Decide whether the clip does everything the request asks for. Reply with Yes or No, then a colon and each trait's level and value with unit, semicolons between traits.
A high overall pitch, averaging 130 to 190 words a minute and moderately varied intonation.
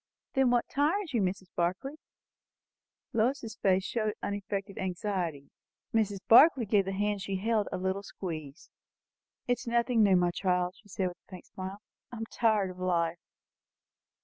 Yes: high, 200 Hz; average, 165 wpm; average, 3.6 semitones